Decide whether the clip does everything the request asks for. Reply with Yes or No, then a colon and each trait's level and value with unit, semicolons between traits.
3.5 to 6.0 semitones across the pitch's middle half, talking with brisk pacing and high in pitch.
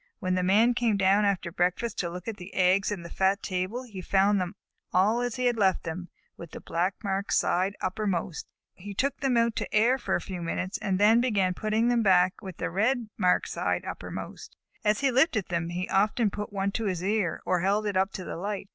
No: average, 3.1 semitones; fast, 225 wpm; high, 195 Hz